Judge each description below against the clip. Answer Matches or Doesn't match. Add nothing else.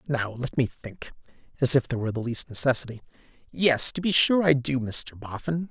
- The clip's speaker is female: Doesn't match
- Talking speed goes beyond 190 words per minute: Matches